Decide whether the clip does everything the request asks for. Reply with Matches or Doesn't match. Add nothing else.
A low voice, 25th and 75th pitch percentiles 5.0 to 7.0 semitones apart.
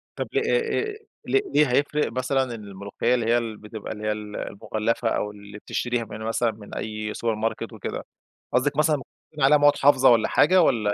Matches